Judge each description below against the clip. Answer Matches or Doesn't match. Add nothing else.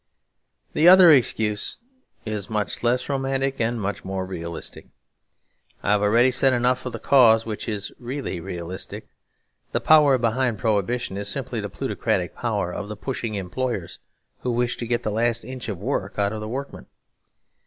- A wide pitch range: Doesn't match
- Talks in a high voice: Doesn't match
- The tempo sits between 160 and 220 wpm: Matches